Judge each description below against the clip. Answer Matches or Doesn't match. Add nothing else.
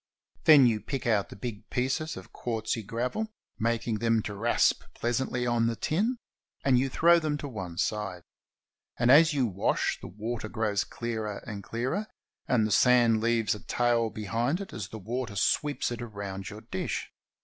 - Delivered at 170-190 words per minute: Matches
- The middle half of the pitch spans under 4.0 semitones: Matches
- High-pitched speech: Doesn't match